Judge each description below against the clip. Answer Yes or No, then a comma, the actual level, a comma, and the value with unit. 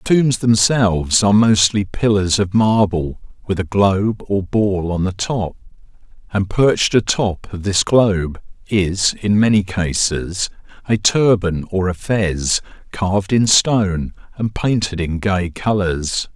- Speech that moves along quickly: No, average, 145 wpm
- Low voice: Yes, low, 100 Hz